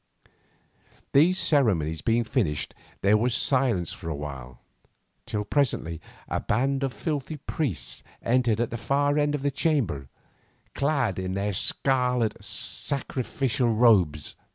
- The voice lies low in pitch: Yes, low, 120 Hz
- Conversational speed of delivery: No, slow, 130 wpm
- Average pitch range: No, wide, 6.7 semitones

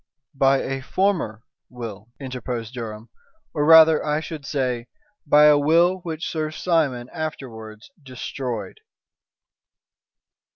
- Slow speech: Yes, slow, 110 wpm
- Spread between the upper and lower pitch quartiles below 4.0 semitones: No, average, 4.6 semitones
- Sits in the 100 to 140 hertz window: Yes, low, 135 Hz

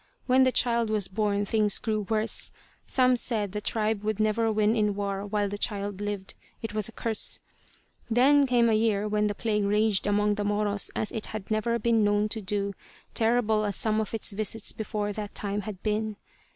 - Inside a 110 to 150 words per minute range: No, average, 200 wpm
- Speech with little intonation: Yes, narrow, 1.4 semitones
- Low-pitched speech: No, high, 215 Hz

